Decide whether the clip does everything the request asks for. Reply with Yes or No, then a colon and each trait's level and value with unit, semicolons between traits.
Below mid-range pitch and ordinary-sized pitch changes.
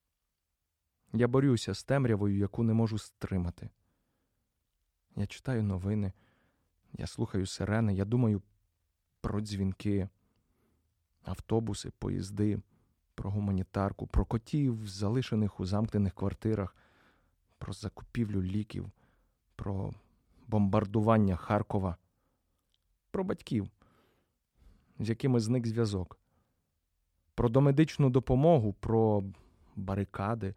Yes: low, 100 Hz; average, 3.4 semitones